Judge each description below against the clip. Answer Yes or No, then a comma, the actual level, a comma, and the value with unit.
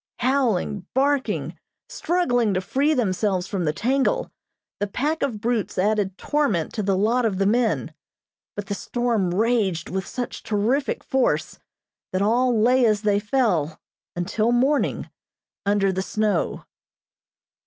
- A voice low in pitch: No, high, 215 Hz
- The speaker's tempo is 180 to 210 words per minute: No, slow, 135 wpm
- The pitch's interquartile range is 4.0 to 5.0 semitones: Yes, average, 4.4 semitones